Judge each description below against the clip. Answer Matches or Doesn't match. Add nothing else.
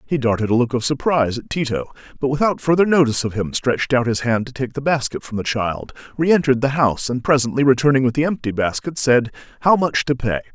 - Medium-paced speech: Doesn't match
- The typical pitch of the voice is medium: Doesn't match